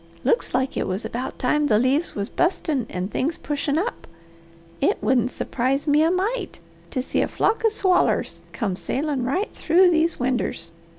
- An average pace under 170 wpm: No, average, 175 wpm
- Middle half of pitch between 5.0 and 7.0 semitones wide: Yes, wide, 5.5 semitones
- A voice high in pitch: Yes, very high, 285 Hz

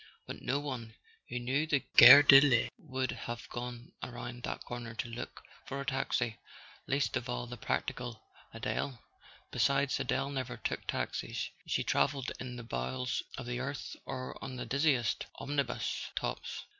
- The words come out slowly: No, average, 160 wpm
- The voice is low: Yes, low, 125 Hz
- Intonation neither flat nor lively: No, narrow, 2.2 semitones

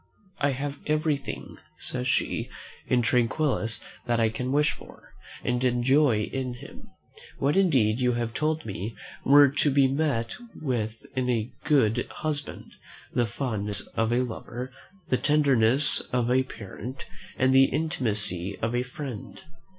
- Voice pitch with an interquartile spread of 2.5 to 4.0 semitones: Yes, average, 3.7 semitones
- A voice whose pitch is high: No, low, 125 Hz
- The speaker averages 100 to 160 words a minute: Yes, average, 145 wpm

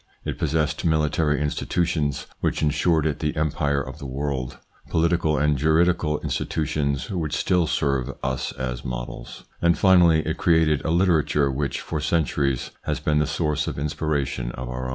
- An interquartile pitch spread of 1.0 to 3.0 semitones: Yes, narrow, 2.5 semitones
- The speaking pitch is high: No, very low, 75 Hz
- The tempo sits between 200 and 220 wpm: No, average, 165 wpm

